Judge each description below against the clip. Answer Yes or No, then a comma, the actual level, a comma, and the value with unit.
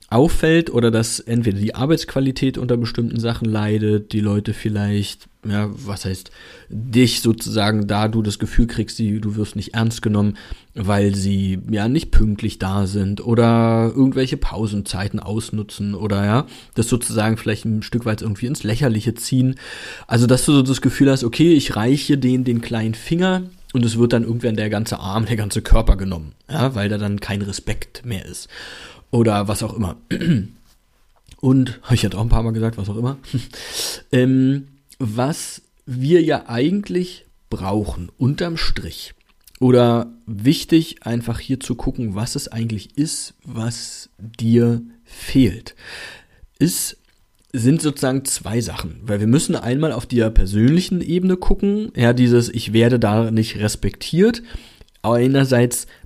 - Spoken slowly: No, average, 155 wpm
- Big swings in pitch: No, average, 3.5 semitones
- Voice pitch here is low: Yes, low, 115 Hz